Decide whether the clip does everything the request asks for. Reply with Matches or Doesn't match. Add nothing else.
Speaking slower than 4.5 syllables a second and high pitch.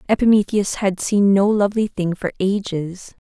Doesn't match